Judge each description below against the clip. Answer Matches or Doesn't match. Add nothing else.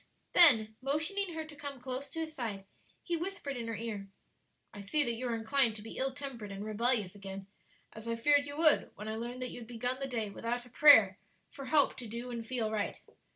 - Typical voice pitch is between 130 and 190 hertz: Doesn't match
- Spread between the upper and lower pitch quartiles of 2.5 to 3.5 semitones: Doesn't match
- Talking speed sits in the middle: Doesn't match